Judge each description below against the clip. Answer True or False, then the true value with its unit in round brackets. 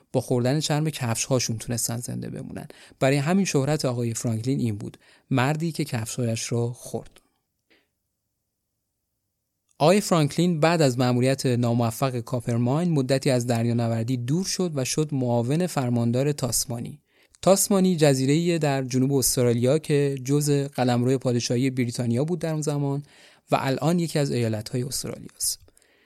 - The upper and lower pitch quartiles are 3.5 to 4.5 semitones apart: True (3.8 semitones)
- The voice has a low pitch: True (130 Hz)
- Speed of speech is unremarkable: True (130 wpm)